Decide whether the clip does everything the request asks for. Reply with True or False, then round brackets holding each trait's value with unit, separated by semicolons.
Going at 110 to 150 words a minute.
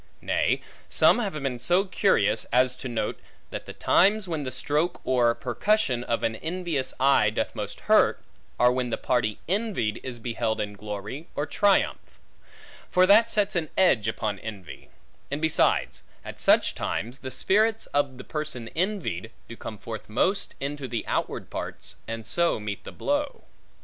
False (165 wpm)